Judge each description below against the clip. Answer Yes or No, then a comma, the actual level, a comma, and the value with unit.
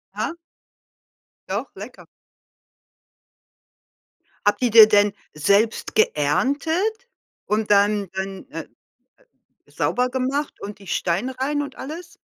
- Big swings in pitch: Yes, wide, 6.0 semitones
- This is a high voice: Yes, high, 220 Hz